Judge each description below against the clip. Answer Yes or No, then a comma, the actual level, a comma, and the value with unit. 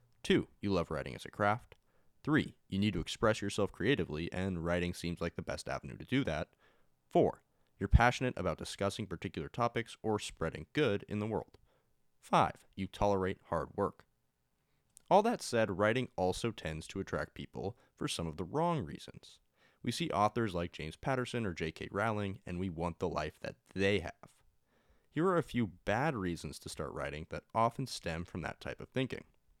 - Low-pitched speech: Yes, very low, 95 Hz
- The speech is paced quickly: No, average, 185 wpm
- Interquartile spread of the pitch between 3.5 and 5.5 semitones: Yes, average, 5.1 semitones